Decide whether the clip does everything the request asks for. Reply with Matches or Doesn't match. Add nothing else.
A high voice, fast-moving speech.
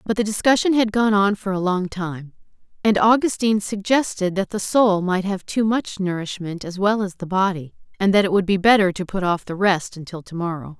Matches